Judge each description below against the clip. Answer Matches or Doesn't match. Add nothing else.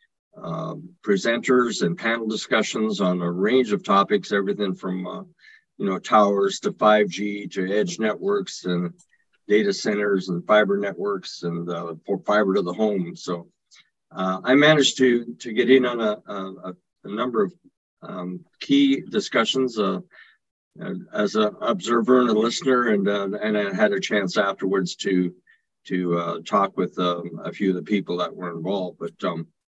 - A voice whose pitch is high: Doesn't match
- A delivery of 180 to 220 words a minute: Doesn't match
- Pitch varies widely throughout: Matches